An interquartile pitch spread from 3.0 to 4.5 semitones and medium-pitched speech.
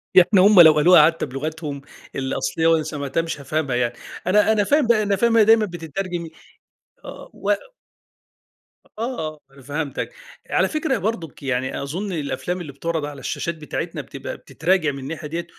No: average, 5.0 semitones; medium, 165 Hz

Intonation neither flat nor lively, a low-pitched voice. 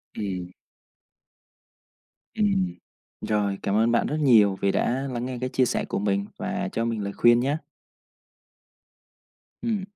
No: wide, 6.4 semitones; low, 120 Hz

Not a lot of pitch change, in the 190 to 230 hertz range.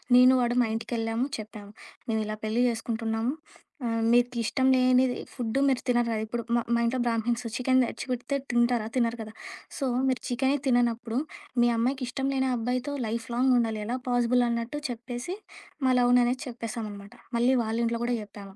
No: narrow, 1.8 semitones; high, 240 Hz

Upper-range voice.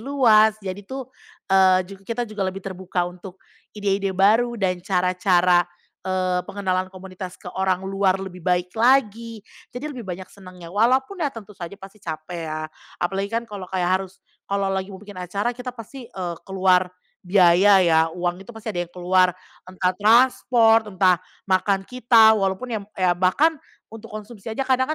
Yes: high, 195 Hz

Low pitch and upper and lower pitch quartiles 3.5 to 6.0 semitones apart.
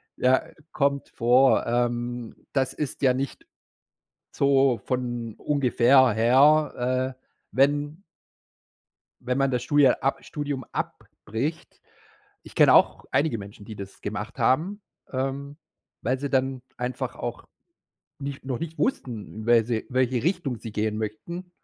No: low, 130 Hz; average, 2.8 semitones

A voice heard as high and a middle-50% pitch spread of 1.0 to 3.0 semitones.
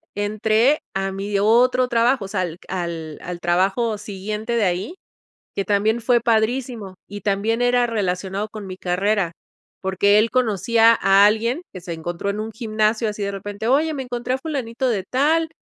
No: high, 215 Hz; average, 3.5 semitones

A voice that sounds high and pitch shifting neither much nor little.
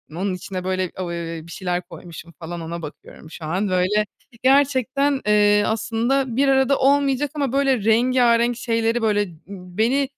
No: high, 220 Hz; wide, 6.2 semitones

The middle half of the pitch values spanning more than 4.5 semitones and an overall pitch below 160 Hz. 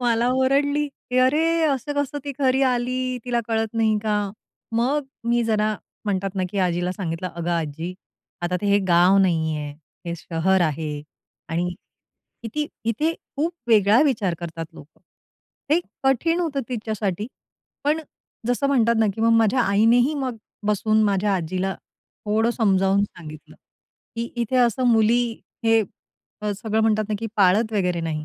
No: average, 4.9 semitones; high, 220 Hz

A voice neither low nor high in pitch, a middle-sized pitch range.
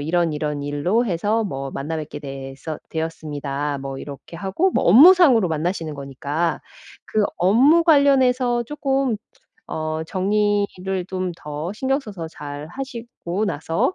No: medium, 175 Hz; wide, 7.9 semitones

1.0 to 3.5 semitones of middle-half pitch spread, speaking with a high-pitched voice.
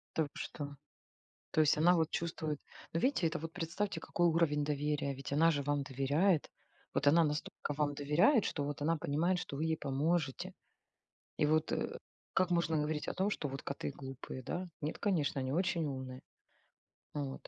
No: average, 2.8 semitones; medium, 150 Hz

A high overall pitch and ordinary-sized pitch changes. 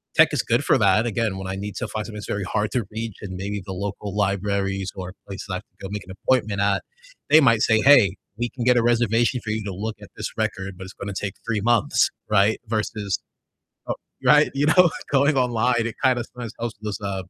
No: low, 105 Hz; average, 3.1 semitones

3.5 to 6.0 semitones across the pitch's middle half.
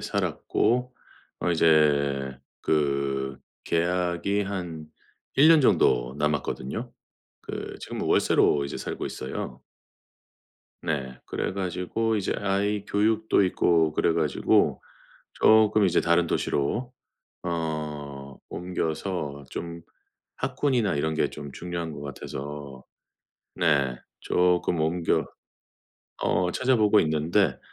Yes: wide, 5.4 semitones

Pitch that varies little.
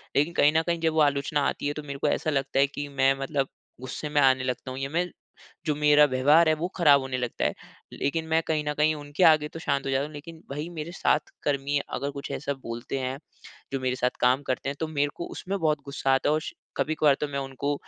Yes: narrow, 2.3 semitones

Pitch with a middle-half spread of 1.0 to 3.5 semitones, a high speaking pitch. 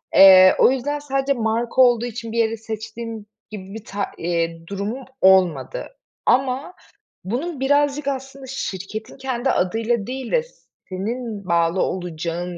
No: wide, 5.6 semitones; high, 225 Hz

